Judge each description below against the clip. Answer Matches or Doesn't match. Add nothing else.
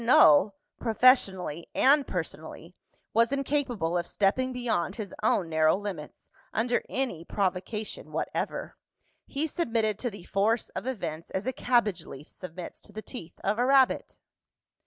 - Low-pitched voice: Doesn't match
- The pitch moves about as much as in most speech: Doesn't match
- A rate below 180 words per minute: Matches